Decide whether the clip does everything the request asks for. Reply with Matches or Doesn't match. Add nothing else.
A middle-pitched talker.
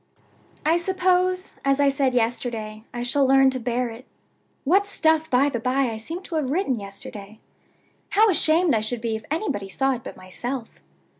Doesn't match